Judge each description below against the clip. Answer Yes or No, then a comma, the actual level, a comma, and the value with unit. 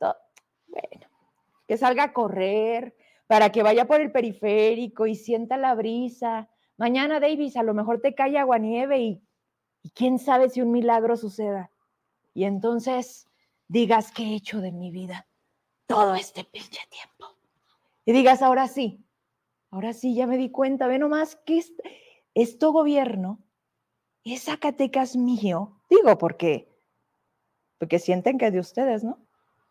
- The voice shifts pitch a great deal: No, average, 3.4 semitones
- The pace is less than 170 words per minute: Yes, average, 150 wpm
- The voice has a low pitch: No, high, 235 Hz